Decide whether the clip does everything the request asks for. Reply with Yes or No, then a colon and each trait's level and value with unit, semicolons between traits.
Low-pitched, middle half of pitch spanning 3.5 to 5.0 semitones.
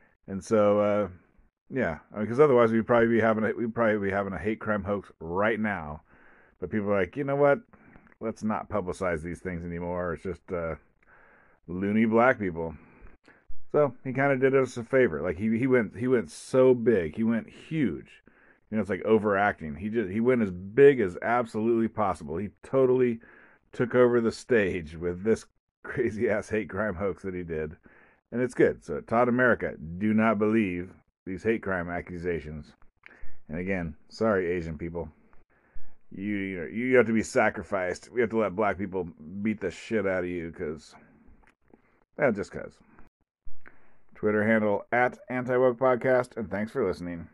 Yes: low, 105 Hz; average, 4.7 semitones